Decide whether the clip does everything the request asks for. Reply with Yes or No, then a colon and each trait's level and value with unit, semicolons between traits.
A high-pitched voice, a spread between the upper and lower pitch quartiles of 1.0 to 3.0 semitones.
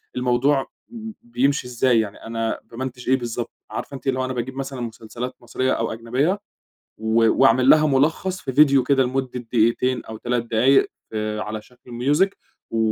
No: low, 125 Hz; narrow, 2.6 semitones